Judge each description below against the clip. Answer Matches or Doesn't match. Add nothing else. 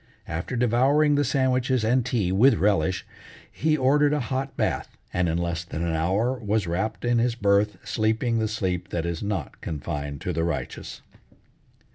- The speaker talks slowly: Doesn't match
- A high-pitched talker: Doesn't match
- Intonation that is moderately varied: Doesn't match